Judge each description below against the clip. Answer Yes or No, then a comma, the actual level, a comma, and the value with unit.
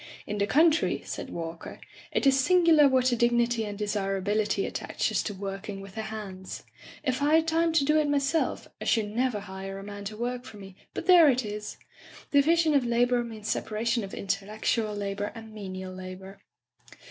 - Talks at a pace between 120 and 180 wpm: No, average, 190 wpm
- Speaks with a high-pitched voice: Yes, high, 220 Hz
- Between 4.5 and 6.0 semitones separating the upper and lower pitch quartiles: Yes, average, 5.0 semitones